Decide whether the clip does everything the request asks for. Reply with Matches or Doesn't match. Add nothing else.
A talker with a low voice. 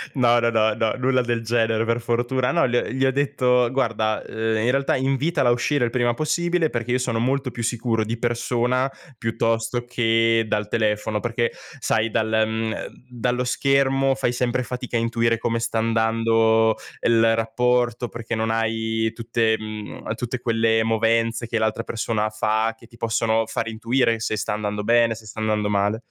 Matches